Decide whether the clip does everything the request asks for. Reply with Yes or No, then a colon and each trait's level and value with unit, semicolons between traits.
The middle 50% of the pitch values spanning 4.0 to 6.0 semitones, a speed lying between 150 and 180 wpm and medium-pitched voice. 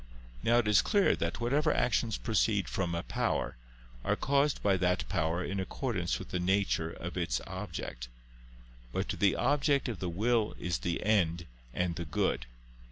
No: wide, 5.6 semitones; average, 165 wpm; very low, 95 Hz